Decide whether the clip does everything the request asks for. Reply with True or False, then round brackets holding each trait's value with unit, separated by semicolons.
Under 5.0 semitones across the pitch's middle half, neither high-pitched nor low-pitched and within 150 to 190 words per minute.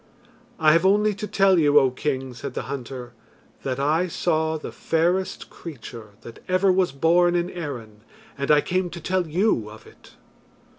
False (5.3 semitones; 160 Hz; 170 wpm)